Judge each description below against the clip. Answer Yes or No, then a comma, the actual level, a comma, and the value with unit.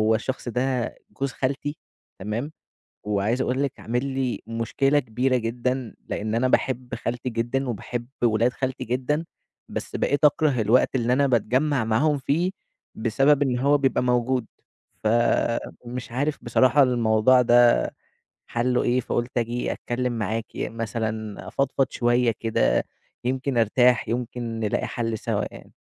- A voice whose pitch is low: Yes, low, 125 Hz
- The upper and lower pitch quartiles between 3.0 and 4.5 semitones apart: No, narrow, 2.4 semitones